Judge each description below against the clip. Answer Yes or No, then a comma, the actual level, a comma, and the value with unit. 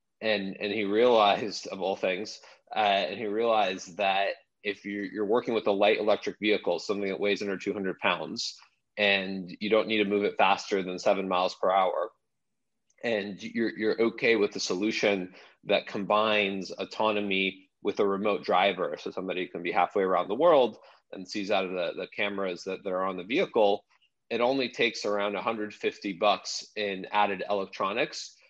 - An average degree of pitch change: No, narrow, 1.5 semitones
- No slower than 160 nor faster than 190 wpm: Yes, average, 175 wpm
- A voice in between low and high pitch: No, low, 100 Hz